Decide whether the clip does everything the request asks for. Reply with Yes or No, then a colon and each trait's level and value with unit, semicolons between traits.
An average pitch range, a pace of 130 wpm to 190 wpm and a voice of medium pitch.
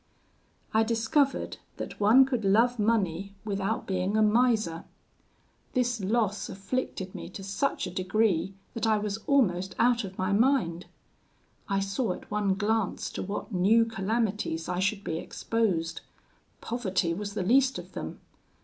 No: average, 3.3 semitones; average, 150 wpm; high, 205 Hz